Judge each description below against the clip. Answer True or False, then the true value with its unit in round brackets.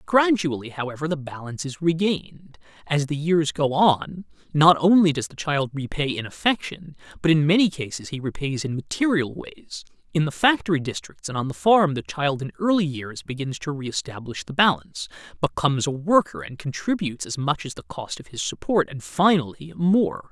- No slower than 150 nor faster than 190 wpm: True (185 wpm)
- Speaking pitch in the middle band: True (155 Hz)